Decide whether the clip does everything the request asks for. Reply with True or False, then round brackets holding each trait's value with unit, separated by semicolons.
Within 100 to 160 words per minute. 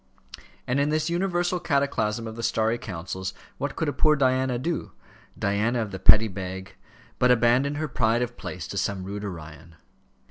False (175 wpm)